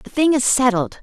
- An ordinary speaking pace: No, fast, 235 wpm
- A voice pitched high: Yes, high, 245 Hz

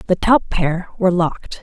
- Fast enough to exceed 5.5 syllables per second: No, 5.1 syllables/s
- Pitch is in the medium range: Yes, medium, 180 Hz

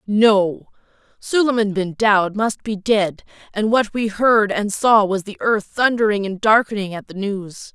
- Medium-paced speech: Yes, average, 170 wpm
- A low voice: No, high, 210 Hz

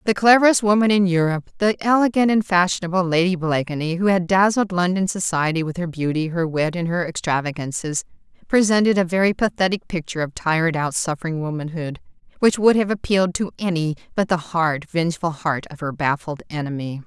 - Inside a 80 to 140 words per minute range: No, average, 170 wpm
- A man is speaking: No, female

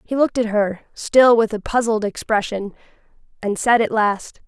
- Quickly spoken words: No, average, 175 wpm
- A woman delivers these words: Yes, female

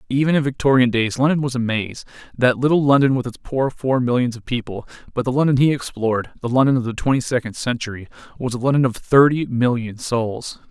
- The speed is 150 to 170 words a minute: No, fast, 205 wpm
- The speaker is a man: Yes, male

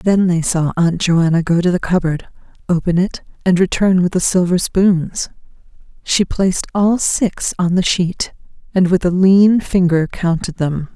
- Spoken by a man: No, female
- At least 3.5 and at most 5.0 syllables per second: Yes, 4.3 syllables/s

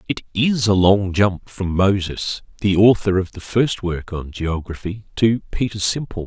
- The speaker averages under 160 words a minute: No, average, 170 wpm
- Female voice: No, male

